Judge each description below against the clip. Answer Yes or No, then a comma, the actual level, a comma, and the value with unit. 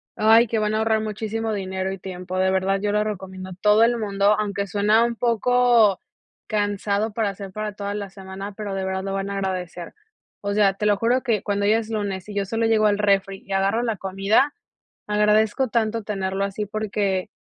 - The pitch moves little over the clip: Yes, narrow, 1.9 semitones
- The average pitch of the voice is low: No, high, 205 Hz